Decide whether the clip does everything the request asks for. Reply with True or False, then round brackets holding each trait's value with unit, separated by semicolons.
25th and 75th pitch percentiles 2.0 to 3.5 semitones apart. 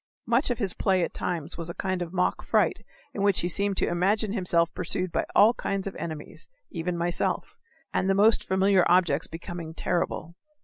True (2.6 semitones)